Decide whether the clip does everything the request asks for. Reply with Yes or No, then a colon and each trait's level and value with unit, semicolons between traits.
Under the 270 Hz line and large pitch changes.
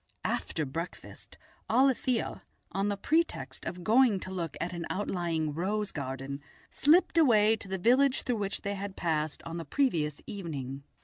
Yes: high, 190 Hz; wide, 5.7 semitones